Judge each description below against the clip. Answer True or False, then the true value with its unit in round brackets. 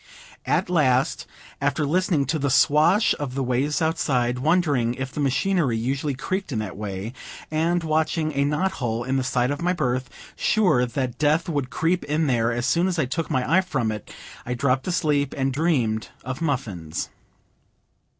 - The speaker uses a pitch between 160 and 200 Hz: False (140 Hz)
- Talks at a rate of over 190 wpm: False (180 wpm)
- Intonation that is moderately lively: True (4.3 semitones)